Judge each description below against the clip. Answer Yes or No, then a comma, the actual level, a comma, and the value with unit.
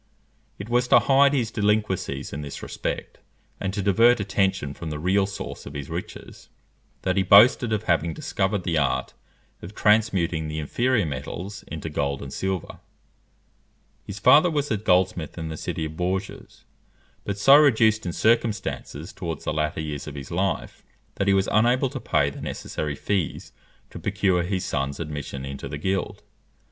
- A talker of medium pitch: No, very low, 95 Hz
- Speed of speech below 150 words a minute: No, average, 170 wpm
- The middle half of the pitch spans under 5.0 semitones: No, wide, 5.4 semitones